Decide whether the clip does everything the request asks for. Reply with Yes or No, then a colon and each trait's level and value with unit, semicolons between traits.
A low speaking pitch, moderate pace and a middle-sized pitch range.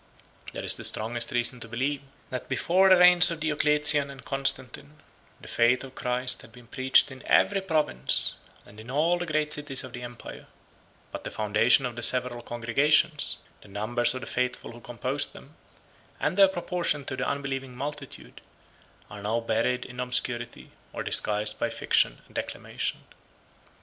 Yes: low, 130 Hz; average, 170 wpm; average, 3.8 semitones